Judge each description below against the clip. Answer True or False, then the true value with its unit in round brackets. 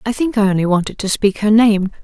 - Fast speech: True (265 wpm)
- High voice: True (210 Hz)